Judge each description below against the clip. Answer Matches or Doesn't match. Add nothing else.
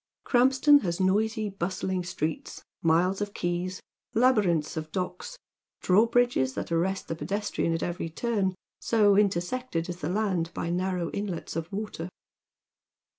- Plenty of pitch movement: Doesn't match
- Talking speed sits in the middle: Doesn't match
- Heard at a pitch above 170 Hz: Matches